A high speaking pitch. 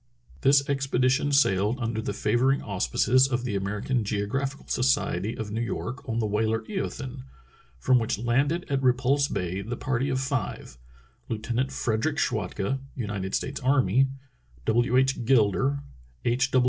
No: low, 125 Hz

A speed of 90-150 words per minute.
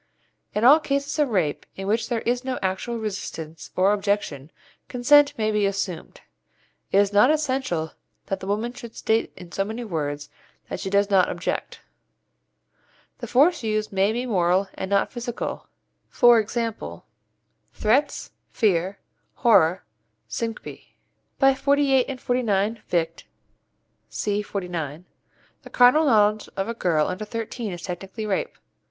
Yes: average, 140 wpm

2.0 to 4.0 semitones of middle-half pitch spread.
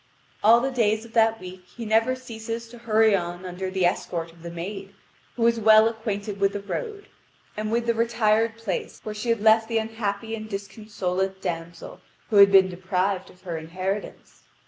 Yes: average, 3.1 semitones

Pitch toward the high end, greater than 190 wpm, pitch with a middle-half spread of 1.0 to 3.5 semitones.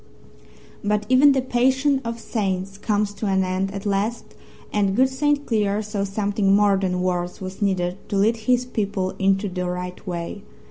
No: high, 205 Hz; average, 175 wpm; average, 3.1 semitones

